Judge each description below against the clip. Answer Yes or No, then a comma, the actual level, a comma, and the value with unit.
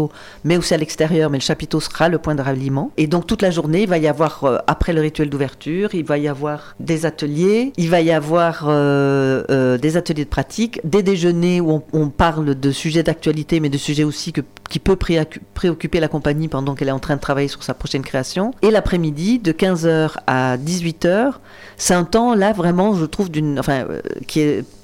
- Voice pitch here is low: No, medium, 155 Hz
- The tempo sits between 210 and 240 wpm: Yes, average, 215 wpm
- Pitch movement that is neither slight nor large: Yes, average, 3.2 semitones